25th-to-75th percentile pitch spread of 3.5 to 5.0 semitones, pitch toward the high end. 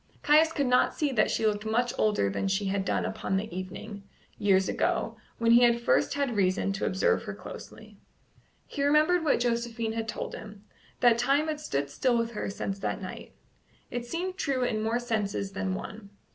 Yes: average, 4.0 semitones; high, 225 Hz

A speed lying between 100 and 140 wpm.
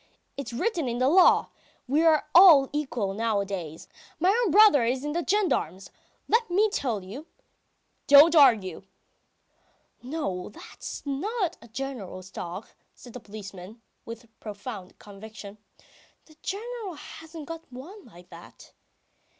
Yes: slow, 135 wpm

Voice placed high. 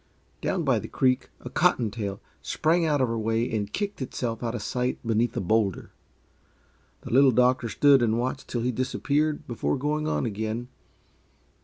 No: low, 120 Hz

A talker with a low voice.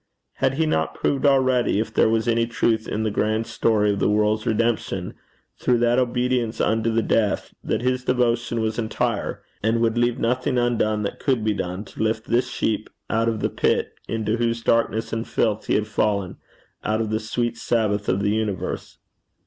Yes: low, 115 Hz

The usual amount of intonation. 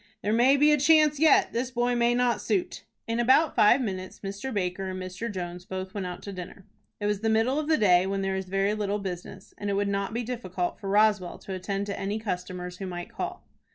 Yes: average, 4.1 semitones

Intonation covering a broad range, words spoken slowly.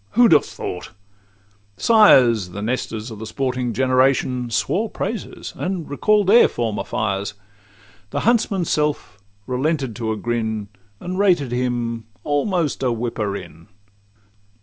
Yes: wide, 6.4 semitones; slow, 130 wpm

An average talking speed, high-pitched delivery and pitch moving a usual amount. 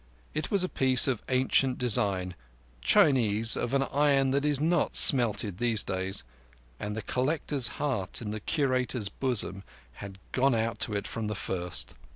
No: average, 165 wpm; low, 120 Hz; average, 4.7 semitones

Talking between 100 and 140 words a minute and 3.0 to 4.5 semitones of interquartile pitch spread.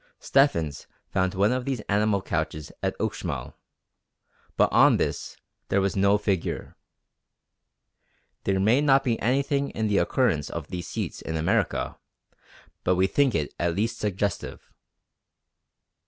No: slow, 135 wpm; wide, 5.6 semitones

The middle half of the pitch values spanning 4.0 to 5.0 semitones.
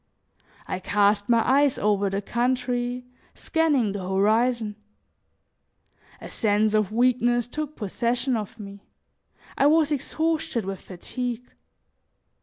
No: average, 3.6 semitones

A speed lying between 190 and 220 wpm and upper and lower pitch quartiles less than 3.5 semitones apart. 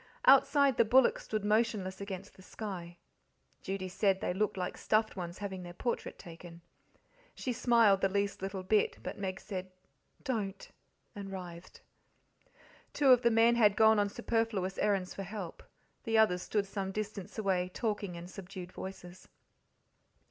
No: average, 155 wpm; average, 2.8 semitones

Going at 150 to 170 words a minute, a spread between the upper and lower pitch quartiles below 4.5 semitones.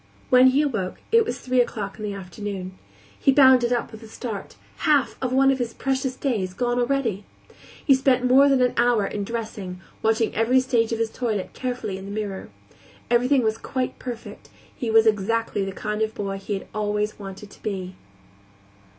No: average, 190 wpm; average, 3.7 semitones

